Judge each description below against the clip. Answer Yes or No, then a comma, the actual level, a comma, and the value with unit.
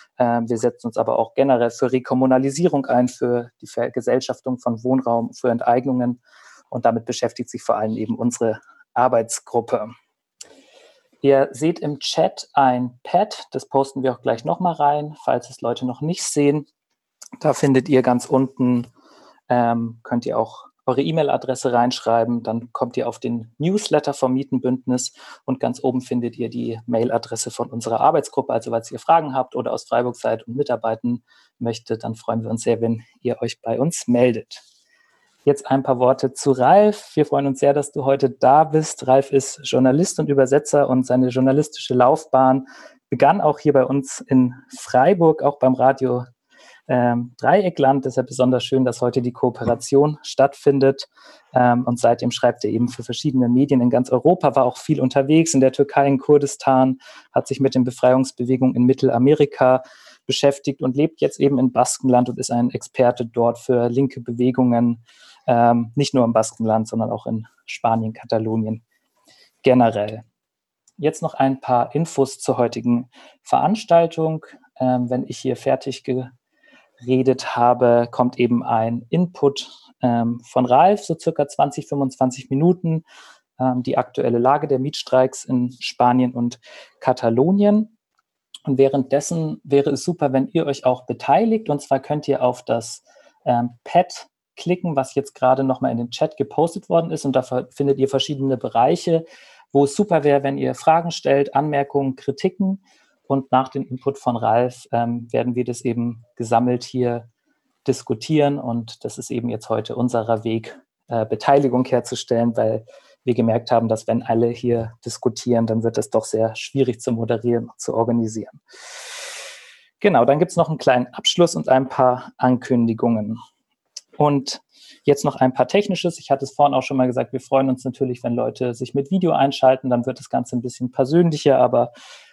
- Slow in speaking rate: No, average, 165 wpm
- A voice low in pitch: Yes, low, 130 Hz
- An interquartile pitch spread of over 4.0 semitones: No, average, 2.8 semitones